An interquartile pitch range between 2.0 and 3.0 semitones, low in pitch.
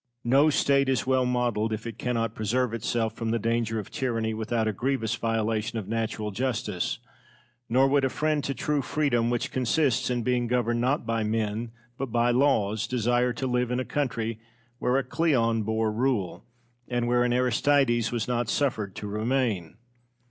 Yes: narrow, 2.5 semitones; low, 120 Hz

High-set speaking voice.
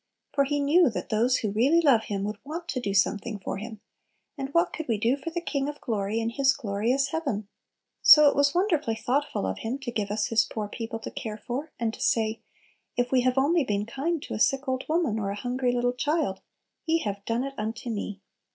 Yes: high, 245 Hz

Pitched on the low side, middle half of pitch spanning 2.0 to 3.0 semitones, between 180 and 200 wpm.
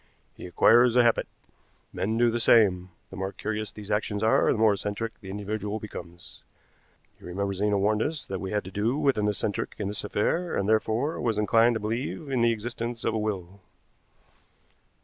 Yes: low, 110 Hz; narrow, 2.4 semitones; average, 190 wpm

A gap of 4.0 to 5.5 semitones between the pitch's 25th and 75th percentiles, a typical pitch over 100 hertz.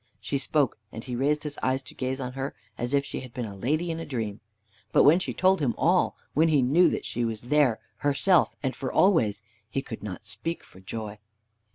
Yes: average, 4.5 semitones; low, 135 Hz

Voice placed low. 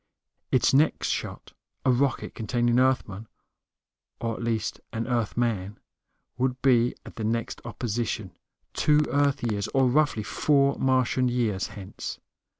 Yes: low, 120 Hz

